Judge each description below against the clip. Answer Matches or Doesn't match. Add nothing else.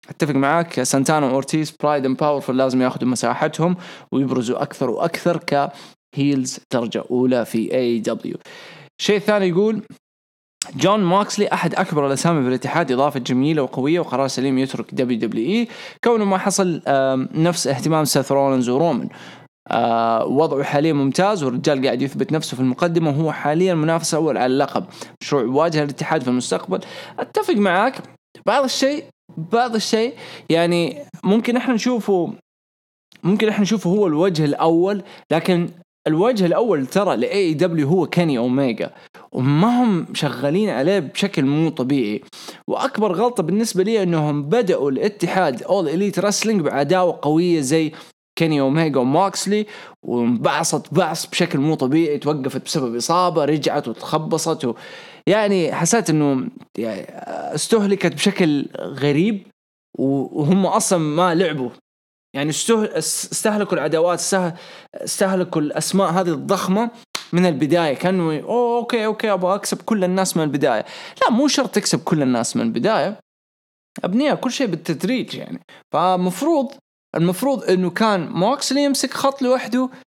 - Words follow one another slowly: Matches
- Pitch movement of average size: Doesn't match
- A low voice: Doesn't match